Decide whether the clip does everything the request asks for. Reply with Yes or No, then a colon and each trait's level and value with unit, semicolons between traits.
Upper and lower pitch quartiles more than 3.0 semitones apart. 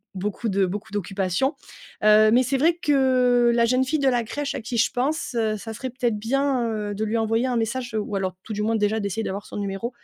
Yes: average, 3.6 semitones